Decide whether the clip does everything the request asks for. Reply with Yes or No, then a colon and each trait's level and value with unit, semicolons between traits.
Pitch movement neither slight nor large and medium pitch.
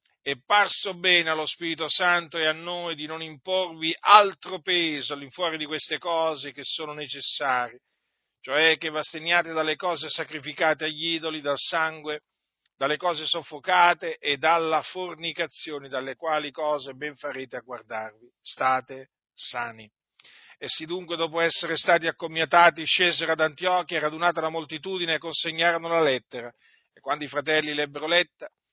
No: narrow, 2.3 semitones; medium, 160 Hz